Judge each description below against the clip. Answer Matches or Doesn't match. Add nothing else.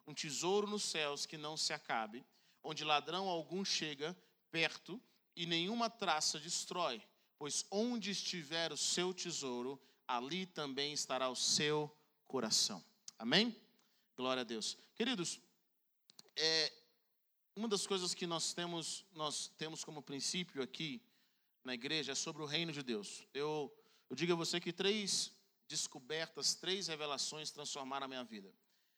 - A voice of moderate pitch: Matches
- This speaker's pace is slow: Doesn't match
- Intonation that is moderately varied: Matches